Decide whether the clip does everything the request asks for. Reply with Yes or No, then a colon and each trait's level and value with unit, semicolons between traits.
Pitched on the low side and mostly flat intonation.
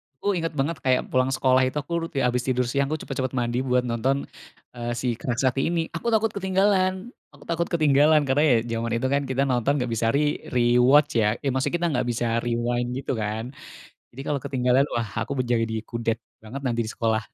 No: low, 130 Hz; average, 3.3 semitones